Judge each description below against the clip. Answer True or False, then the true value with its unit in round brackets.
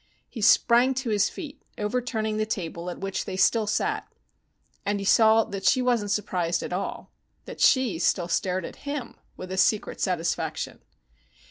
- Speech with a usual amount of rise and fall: True (4.1 semitones)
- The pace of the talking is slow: False (165 wpm)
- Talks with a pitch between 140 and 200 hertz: False (210 Hz)